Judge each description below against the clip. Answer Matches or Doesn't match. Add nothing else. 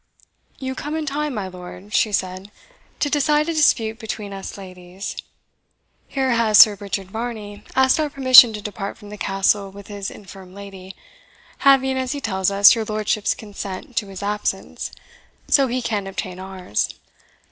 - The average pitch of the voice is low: Doesn't match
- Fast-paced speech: Doesn't match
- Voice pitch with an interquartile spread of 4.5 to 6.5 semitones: Matches